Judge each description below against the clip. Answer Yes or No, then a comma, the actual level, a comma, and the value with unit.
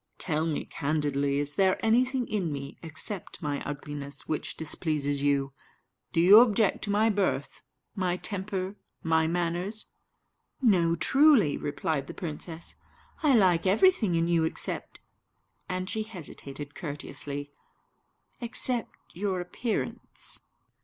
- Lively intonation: Yes, wide, 5.8 semitones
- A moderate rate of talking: No, slow, 120 wpm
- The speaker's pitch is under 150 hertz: No, medium, 175 Hz